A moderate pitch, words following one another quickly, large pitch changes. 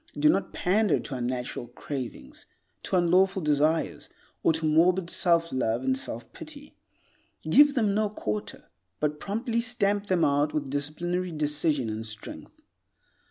No: medium, 160 Hz; average, 140 wpm; wide, 5.7 semitones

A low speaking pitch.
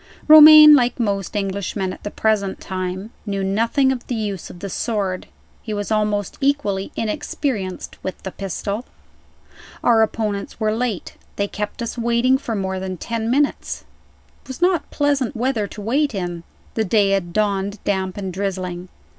No: high, 210 Hz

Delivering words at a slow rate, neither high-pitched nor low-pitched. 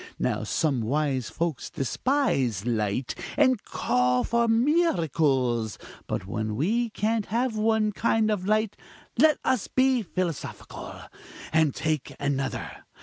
Yes: slow, 120 wpm; medium, 170 Hz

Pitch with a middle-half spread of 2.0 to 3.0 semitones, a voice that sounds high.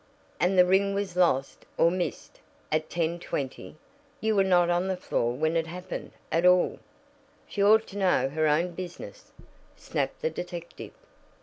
No: narrow, 2.6 semitones; medium, 180 Hz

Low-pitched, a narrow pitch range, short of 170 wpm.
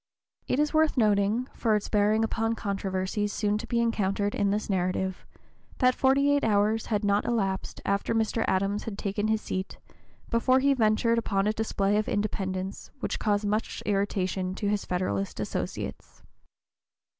No: high, 210 Hz; narrow, 2.3 semitones; average, 160 wpm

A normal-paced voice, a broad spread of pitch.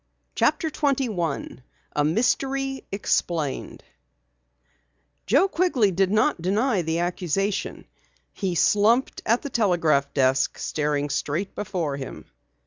No: slow, 105 wpm; wide, 7.3 semitones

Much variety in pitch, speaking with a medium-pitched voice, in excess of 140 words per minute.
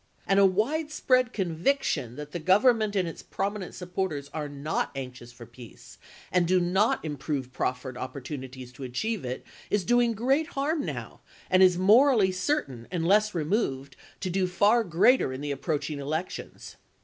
Yes: wide, 7.3 semitones; medium, 180 Hz; average, 160 wpm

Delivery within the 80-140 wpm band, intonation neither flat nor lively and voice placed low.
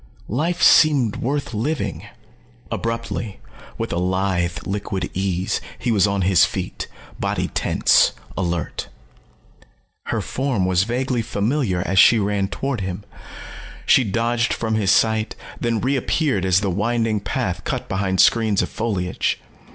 Yes: slow, 135 wpm; average, 3.8 semitones; low, 105 Hz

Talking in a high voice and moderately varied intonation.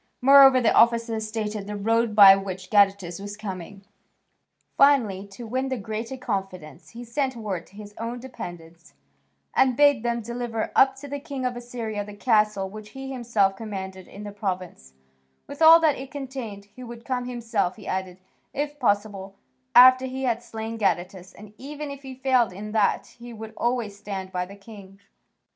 Yes: high, 220 Hz; average, 4.2 semitones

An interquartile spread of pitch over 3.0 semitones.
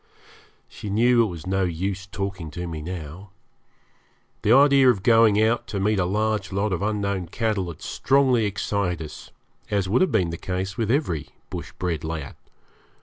Yes: average, 3.6 semitones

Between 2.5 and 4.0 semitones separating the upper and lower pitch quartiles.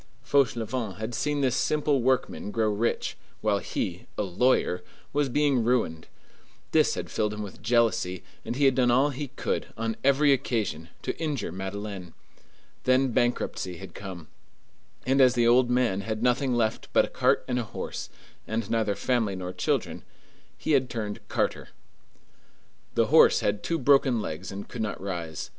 No: average, 4.4 semitones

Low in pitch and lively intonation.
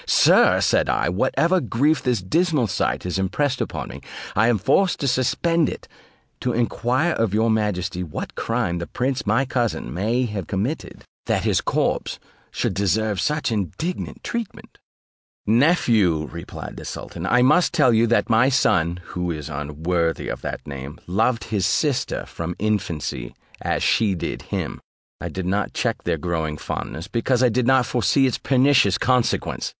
Yes: low, 110 Hz; wide, 6.2 semitones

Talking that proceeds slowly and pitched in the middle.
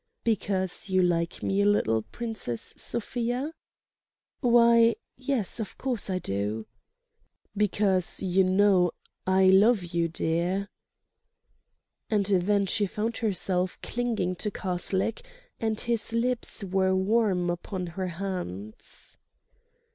No: slow, 105 wpm; high, 195 Hz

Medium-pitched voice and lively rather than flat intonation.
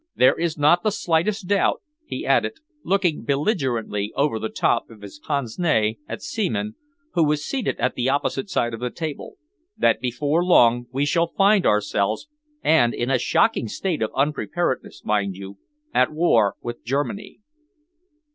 Yes: medium, 145 Hz; wide, 6.7 semitones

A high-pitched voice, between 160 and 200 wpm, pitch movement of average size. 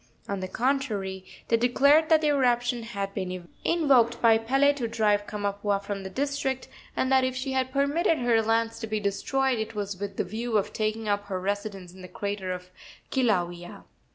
Yes: high, 225 Hz; average, 190 wpm; average, 4.6 semitones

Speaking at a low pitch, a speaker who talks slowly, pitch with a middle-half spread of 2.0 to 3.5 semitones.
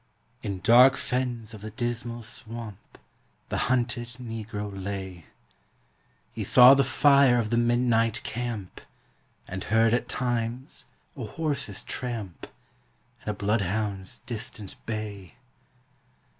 Yes: low, 115 Hz; slow, 115 wpm; average, 2.8 semitones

